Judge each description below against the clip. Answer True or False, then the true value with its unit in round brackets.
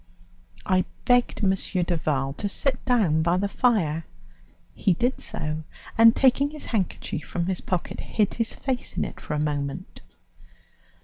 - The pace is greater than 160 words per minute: False (150 wpm)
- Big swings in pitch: True (7.0 semitones)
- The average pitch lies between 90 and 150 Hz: False (190 Hz)